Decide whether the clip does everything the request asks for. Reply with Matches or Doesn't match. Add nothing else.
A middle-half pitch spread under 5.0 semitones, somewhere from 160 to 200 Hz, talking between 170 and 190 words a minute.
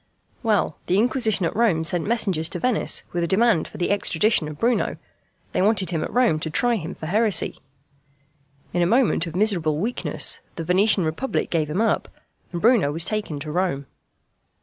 Doesn't match